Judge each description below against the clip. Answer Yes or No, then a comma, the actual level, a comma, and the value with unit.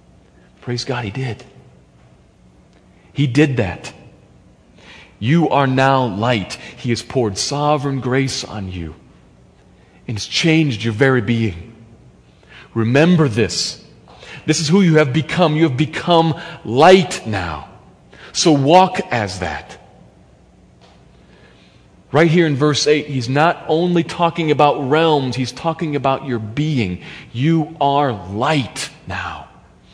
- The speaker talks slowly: Yes, slow, 120 wpm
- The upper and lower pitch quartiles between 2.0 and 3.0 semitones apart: No, wide, 5.6 semitones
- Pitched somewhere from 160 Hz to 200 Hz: No, low, 135 Hz